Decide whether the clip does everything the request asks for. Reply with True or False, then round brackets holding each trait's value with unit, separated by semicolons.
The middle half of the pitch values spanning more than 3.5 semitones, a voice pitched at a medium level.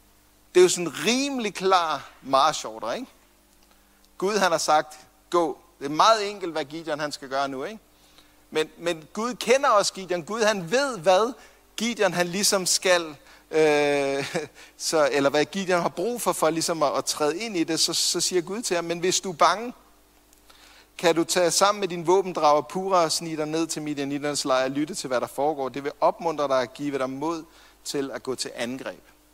True (4.2 semitones; 165 Hz)